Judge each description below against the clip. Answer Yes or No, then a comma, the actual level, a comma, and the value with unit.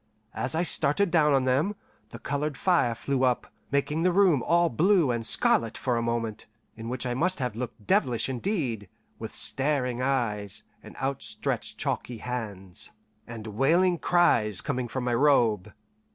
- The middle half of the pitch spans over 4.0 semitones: Yes, average, 4.6 semitones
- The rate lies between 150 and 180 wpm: Yes, average, 160 wpm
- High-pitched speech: No, low, 130 Hz